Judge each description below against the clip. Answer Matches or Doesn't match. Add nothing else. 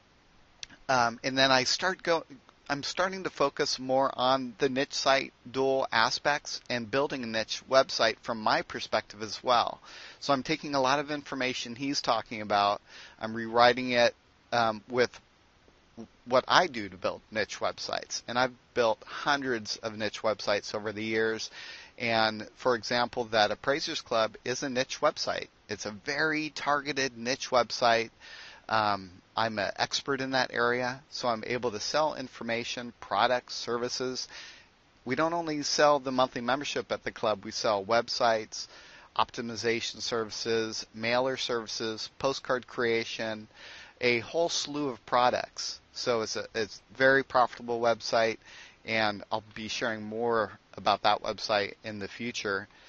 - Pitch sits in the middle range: Doesn't match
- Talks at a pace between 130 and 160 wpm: Matches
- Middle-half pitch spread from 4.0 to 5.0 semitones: Doesn't match